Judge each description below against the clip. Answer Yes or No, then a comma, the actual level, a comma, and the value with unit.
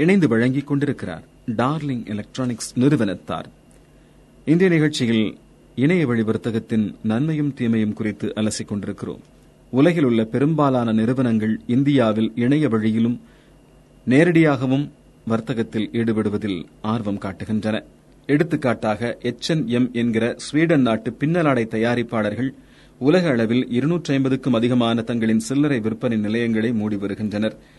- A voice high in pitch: No, low, 115 Hz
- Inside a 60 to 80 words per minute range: No, average, 90 wpm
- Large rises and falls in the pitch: No, average, 3.6 semitones